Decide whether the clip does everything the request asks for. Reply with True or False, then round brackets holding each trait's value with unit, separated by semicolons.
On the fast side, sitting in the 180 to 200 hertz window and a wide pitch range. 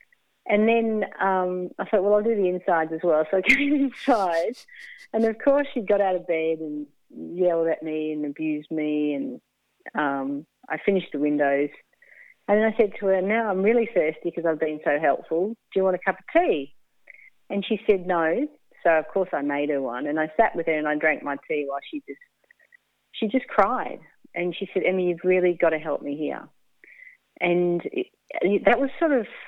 True (210 wpm; 185 Hz; 6.6 semitones)